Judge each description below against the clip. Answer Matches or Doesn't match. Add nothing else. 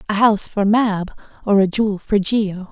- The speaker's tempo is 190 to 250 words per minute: Matches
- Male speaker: Doesn't match